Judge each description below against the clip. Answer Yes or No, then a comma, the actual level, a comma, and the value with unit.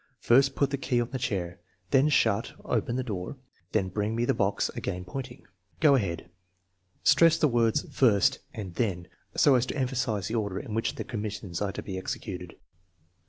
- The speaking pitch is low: Yes, low, 110 Hz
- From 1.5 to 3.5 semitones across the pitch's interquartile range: No, average, 4.8 semitones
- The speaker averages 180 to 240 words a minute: Yes, average, 190 wpm